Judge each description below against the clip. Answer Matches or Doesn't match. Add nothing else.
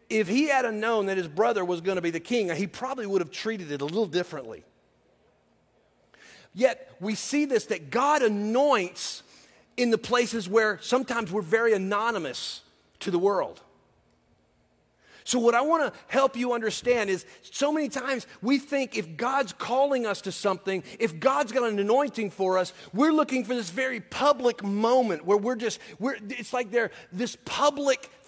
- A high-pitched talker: Matches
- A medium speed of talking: Matches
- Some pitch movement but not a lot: Matches